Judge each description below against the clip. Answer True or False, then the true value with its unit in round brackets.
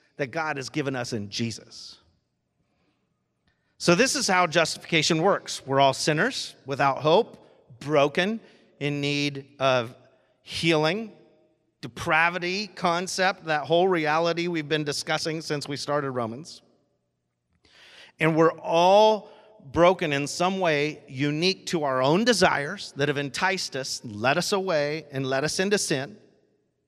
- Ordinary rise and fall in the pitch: True (4.3 semitones)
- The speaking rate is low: True (130 wpm)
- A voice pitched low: False (155 Hz)